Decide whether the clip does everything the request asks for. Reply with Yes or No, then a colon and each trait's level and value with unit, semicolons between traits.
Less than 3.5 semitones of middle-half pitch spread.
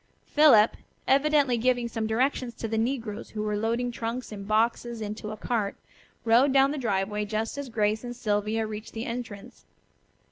Yes: narrow, 2.6 semitones